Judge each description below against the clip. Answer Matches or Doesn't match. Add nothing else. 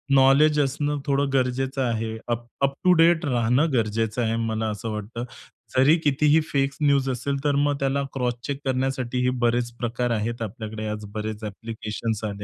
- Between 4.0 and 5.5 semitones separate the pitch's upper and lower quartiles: Doesn't match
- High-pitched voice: Doesn't match